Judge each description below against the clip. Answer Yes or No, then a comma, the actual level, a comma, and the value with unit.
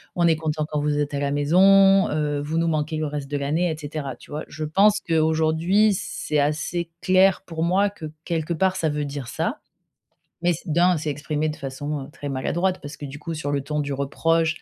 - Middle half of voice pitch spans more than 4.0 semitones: No, average, 2.7 semitones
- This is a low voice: No, medium, 155 Hz